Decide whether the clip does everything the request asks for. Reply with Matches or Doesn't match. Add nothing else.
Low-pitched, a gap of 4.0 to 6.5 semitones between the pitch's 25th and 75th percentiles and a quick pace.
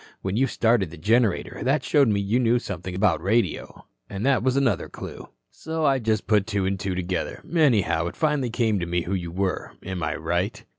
Matches